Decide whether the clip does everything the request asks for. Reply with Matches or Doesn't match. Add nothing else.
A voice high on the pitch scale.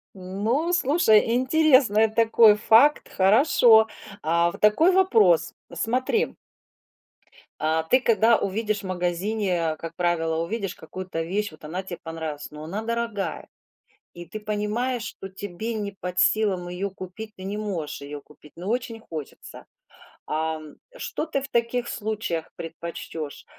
Matches